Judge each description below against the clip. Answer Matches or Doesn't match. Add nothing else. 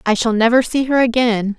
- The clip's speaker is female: Matches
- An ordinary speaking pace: Doesn't match